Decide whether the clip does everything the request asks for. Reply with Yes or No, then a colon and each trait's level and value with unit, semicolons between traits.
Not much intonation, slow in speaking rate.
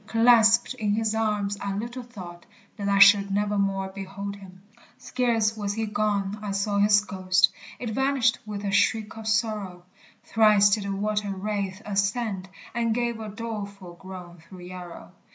No: narrow, 2.1 semitones; average, 160 wpm